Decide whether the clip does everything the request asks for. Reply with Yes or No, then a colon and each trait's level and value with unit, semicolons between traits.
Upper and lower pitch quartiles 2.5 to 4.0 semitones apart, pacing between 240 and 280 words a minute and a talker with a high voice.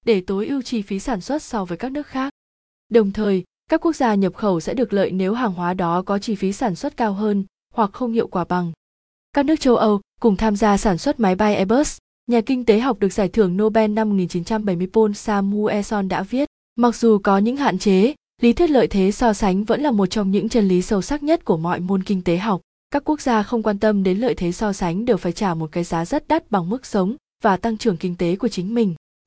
Yes: average, 3.6 semitones; fast, 250 wpm; high, 215 Hz